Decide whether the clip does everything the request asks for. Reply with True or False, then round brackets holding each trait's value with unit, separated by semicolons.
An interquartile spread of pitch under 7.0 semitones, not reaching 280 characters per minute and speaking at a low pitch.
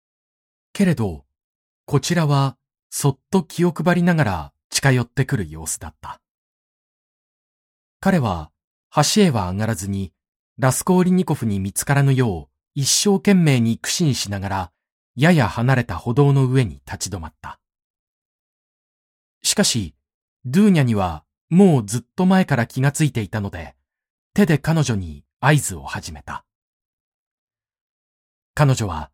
False (8.1 semitones; 250 characters per minute; 125 Hz)